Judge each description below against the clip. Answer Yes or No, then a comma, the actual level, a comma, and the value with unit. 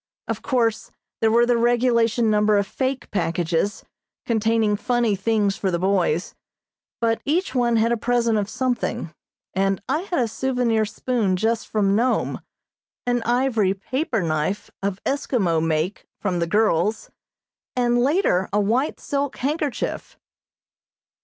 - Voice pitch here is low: No, high, 225 Hz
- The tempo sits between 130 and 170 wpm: Yes, average, 140 wpm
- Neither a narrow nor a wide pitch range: Yes, average, 3.7 semitones